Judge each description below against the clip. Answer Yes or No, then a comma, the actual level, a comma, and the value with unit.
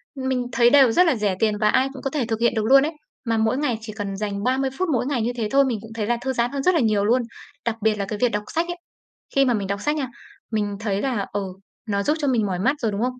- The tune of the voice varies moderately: Yes, average, 4.0 semitones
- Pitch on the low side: No, high, 235 Hz